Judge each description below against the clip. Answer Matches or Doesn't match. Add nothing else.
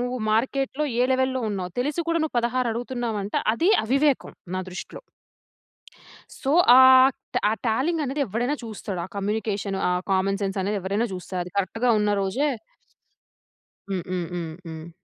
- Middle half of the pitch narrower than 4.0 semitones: Doesn't match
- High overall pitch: Matches